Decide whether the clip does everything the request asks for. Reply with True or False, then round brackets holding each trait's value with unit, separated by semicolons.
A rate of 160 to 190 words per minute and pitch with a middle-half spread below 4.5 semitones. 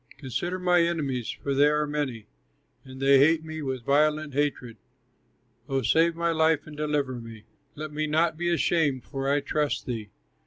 True (170 wpm; 2.9 semitones)